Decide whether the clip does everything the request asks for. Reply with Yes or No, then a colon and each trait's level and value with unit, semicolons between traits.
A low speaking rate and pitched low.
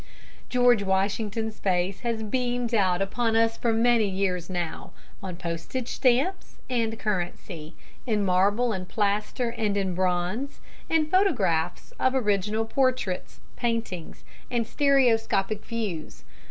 No: slow, 125 wpm; high, 215 Hz